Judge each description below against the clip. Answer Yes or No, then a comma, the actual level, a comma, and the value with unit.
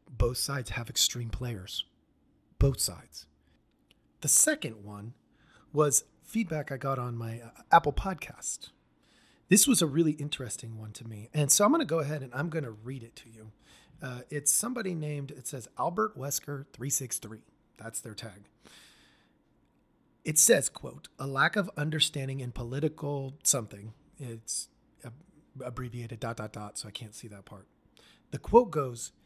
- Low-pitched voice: Yes, low, 130 Hz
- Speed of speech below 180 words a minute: Yes, average, 160 wpm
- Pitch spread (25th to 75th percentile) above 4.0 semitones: Yes, average, 4.6 semitones